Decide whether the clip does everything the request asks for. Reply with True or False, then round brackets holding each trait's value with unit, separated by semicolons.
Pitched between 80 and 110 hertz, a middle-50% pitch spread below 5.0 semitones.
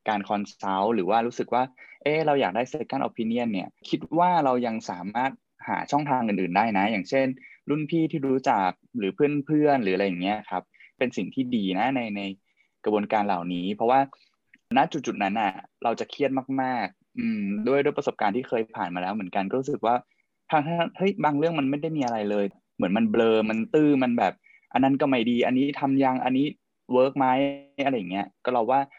False (135 Hz; 4.5 semitones)